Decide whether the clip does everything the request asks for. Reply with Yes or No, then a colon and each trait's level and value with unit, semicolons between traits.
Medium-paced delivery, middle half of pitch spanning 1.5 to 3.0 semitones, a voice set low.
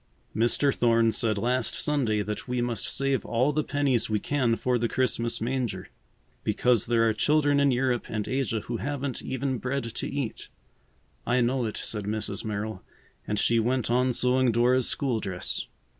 Yes: average, 175 wpm; average, 2.7 semitones; low, 120 Hz